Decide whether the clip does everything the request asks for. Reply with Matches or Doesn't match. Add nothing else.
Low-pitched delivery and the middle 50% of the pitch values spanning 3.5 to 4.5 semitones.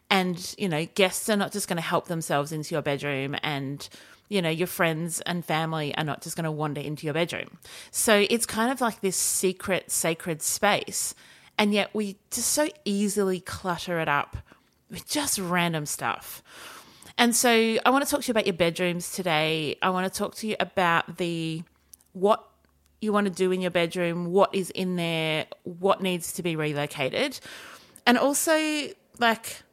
Doesn't match